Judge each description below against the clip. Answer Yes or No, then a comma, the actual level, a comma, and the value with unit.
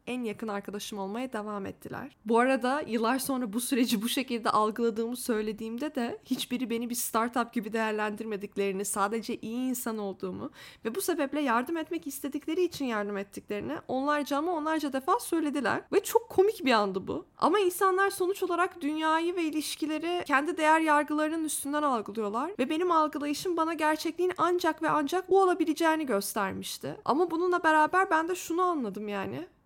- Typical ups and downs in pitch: No, wide, 6.1 semitones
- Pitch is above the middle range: Yes, very high, 285 Hz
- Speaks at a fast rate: Yes, fast, 160 wpm